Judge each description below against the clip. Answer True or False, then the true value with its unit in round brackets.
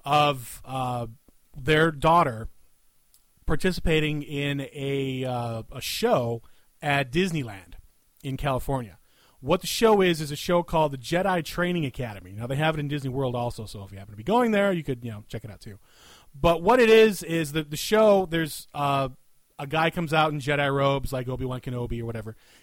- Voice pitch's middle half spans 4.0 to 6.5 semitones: True (5.1 semitones)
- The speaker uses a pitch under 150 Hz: True (140 Hz)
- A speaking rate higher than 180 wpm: True (195 wpm)